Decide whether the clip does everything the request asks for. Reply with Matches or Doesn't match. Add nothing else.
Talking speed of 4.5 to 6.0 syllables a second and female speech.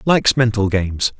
Doesn't match